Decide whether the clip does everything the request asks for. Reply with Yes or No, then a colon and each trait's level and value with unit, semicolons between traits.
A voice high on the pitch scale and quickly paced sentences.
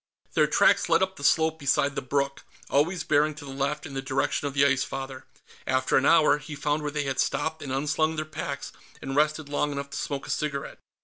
No: medium, 145 Hz; fast, 230 wpm